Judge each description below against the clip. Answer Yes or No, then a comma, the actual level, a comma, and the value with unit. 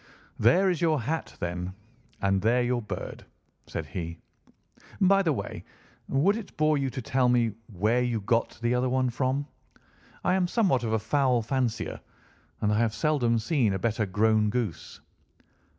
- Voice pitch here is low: Yes, low, 120 Hz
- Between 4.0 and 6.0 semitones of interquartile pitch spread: Yes, average, 4.4 semitones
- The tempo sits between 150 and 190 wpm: Yes, average, 165 wpm